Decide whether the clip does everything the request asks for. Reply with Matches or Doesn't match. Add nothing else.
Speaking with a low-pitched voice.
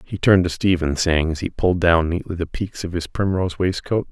Matches